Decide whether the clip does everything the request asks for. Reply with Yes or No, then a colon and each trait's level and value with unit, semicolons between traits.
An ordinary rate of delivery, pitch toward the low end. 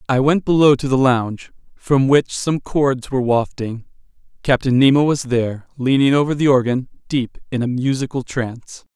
Yes: average, 170 wpm; low, 130 Hz